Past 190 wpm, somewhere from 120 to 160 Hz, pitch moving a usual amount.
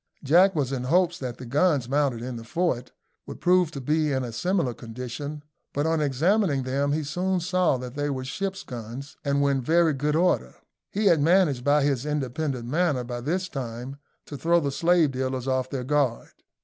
Yes: average, 200 wpm; medium, 140 Hz; average, 4.5 semitones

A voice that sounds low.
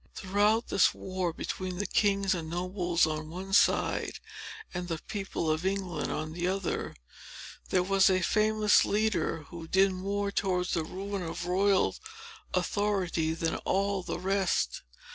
No: medium, 185 Hz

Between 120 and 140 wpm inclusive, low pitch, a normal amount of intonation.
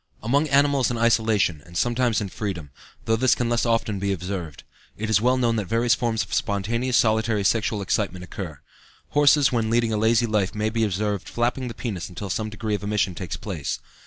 No: average, 200 wpm; low, 110 Hz; average, 3.1 semitones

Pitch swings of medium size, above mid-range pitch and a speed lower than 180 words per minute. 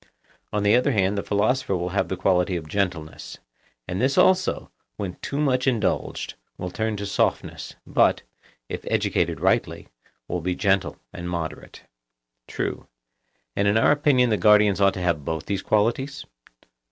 No: average, 4.6 semitones; low, 100 Hz; average, 160 wpm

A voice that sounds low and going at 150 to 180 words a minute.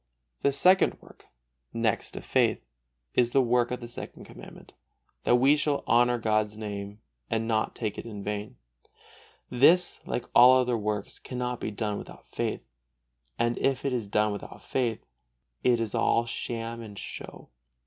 Yes: low, 115 Hz; average, 165 wpm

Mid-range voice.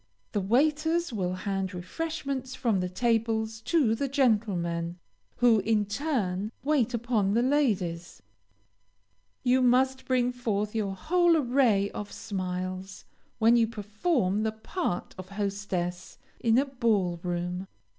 No: high, 220 Hz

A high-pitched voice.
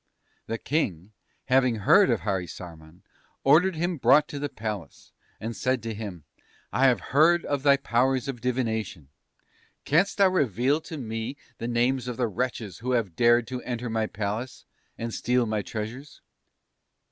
No: low, 120 Hz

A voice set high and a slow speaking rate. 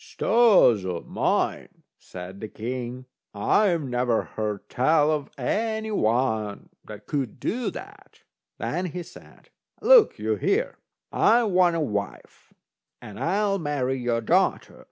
No: low, 135 Hz; slow, 130 wpm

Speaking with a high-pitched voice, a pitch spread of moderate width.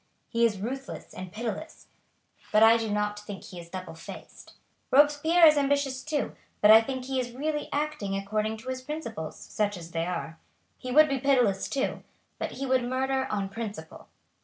Yes: high, 235 Hz; average, 5.0 semitones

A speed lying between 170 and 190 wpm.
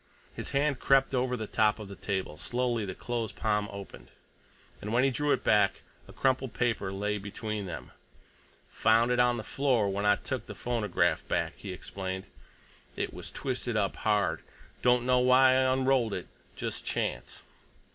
Yes: average, 175 wpm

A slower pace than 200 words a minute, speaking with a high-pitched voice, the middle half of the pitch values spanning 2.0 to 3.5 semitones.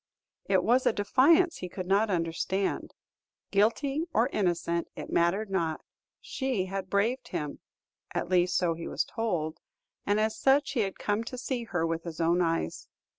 No: average, 170 wpm; high, 195 Hz; average, 5.1 semitones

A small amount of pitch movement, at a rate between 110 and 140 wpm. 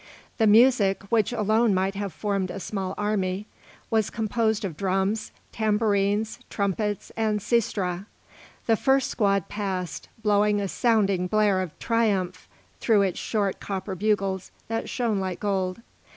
Yes: narrow, 2.3 semitones; slow, 135 wpm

